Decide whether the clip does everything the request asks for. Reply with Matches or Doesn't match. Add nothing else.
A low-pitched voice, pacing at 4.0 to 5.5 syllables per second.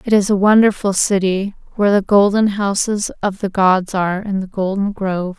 Doesn't match